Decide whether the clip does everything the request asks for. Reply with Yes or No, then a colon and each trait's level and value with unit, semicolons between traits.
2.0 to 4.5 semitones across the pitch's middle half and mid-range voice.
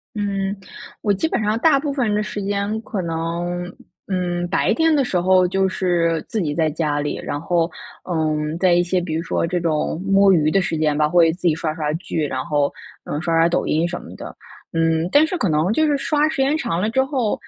Yes: average, 4.2 semitones; medium, 175 Hz